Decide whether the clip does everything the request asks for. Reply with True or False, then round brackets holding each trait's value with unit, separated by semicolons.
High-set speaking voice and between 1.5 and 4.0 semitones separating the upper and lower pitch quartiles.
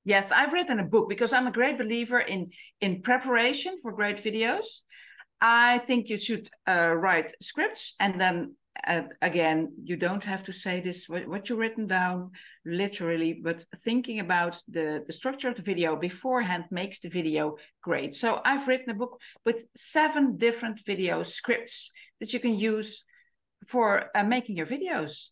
False (215 Hz; 5.3 semitones)